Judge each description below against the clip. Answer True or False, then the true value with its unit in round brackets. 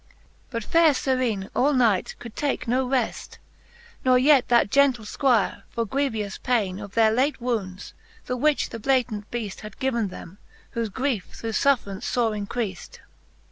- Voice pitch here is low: False (235 Hz)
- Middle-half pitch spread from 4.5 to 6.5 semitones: False (3.9 semitones)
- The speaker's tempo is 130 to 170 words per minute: True (160 wpm)